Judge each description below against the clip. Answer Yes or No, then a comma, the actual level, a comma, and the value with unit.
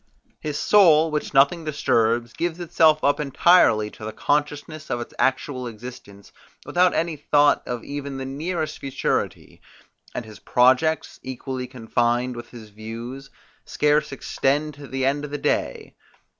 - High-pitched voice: No, low, 135 Hz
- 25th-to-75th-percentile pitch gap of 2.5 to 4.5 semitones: Yes, average, 3.8 semitones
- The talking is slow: No, average, 145 wpm